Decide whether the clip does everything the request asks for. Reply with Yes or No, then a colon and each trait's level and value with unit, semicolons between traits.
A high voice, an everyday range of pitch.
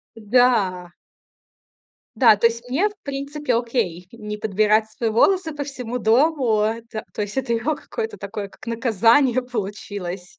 Yes: high, 230 Hz; average, 3.6 semitones